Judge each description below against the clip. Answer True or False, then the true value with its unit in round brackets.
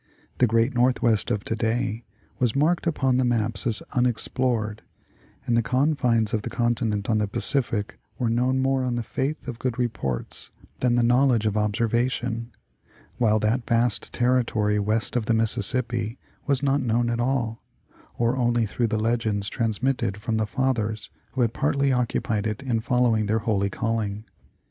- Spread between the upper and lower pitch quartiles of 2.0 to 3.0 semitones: True (2.4 semitones)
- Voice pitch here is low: True (115 Hz)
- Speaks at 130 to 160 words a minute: False (170 wpm)